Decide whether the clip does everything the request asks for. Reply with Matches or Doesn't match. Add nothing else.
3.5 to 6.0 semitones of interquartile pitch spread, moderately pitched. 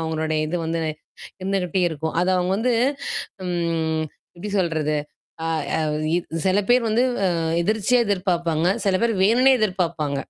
Matches